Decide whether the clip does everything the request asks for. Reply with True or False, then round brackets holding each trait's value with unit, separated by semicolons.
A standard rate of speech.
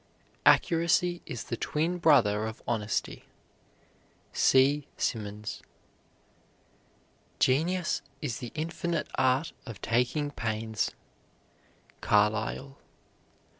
False (80 wpm)